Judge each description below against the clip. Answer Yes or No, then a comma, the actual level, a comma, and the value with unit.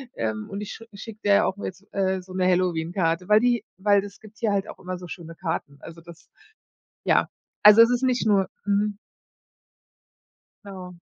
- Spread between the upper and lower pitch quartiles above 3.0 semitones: No, narrow, 2.6 semitones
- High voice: Yes, high, 195 Hz